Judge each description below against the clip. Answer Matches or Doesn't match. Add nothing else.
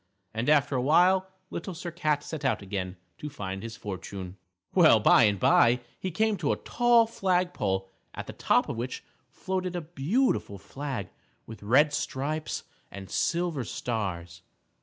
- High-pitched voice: Doesn't match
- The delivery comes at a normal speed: Matches